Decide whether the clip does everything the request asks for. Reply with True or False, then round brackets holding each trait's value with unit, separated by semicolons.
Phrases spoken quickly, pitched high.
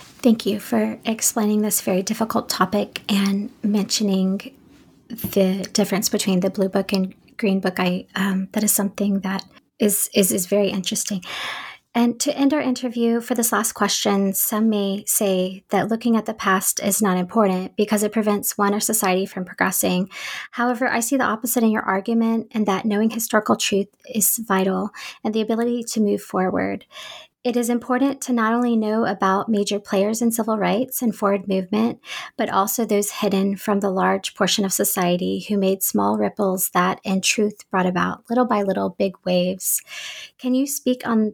False (180 wpm; 205 Hz)